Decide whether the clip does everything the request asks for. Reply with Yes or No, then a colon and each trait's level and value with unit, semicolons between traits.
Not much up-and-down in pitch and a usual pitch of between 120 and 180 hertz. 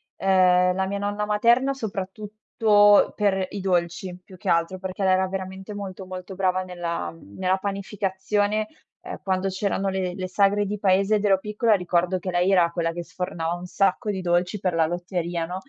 No: narrow, 2.1 semitones; high, 190 Hz